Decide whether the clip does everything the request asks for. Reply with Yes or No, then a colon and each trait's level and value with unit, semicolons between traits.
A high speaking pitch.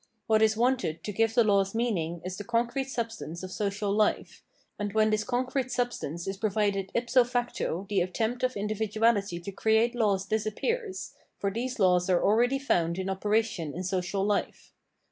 Yes: high, 215 Hz